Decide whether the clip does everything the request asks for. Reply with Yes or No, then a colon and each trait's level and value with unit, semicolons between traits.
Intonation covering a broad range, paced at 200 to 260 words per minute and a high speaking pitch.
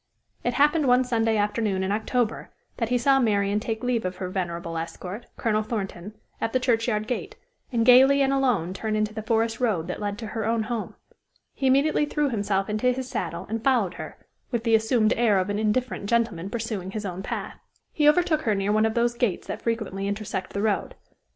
No: average, 3.3 semitones; fast, 205 wpm; high, 220 Hz